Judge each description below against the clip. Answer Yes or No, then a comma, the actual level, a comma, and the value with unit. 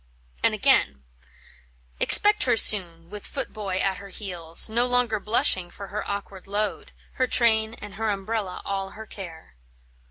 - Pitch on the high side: Yes, high, 200 Hz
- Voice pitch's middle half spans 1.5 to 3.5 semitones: Yes, average, 2.8 semitones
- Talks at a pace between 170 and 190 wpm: No, average, 150 wpm